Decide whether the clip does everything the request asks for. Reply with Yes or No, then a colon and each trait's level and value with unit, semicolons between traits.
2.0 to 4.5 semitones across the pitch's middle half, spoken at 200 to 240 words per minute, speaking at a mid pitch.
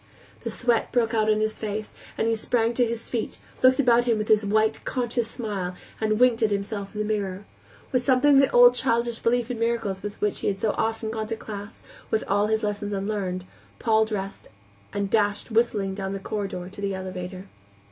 No: narrow, 2.5 semitones; fast, 205 wpm; high, 215 Hz